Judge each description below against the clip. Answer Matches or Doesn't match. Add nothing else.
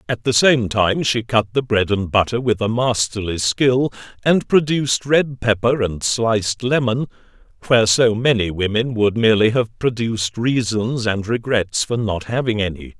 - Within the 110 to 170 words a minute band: Matches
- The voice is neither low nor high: Doesn't match